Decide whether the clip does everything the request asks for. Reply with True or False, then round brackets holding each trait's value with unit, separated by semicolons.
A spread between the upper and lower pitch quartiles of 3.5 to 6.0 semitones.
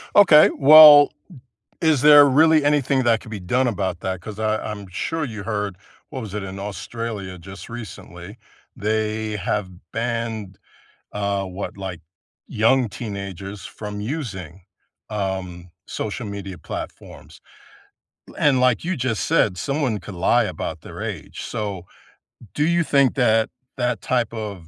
True (4.8 semitones)